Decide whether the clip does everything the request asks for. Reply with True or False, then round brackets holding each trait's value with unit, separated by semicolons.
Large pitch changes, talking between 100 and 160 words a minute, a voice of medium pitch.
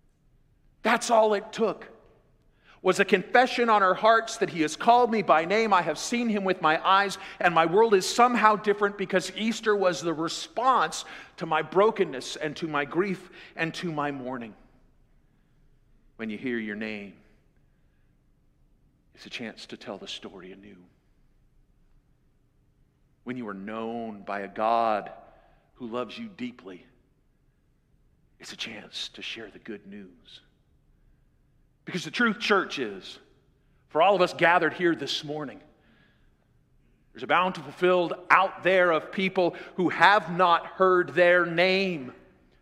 True (5.8 semitones; 150 wpm; 180 Hz)